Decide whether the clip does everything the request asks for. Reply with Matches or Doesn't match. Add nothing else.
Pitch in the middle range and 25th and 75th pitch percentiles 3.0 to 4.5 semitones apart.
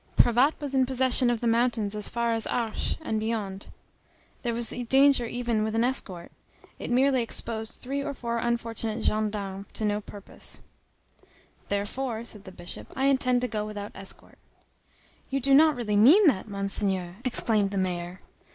Doesn't match